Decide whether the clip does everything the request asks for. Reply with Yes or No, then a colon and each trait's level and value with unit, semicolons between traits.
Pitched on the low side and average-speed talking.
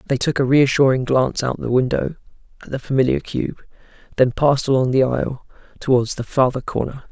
Yes: low, 130 Hz; average, 175 wpm